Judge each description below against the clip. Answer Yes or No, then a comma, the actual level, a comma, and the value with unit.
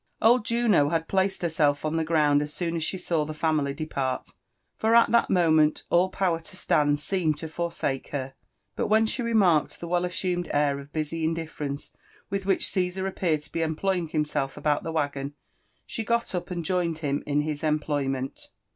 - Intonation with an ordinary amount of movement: Yes, average, 3.6 semitones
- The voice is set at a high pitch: No, medium, 160 Hz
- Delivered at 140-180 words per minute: No, average, 195 wpm